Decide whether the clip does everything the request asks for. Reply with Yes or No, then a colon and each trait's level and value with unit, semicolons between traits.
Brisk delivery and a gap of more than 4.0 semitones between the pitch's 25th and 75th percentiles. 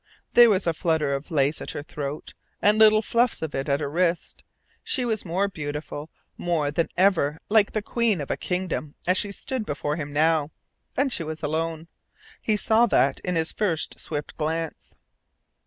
No: average, 185 wpm; wide, 5.5 semitones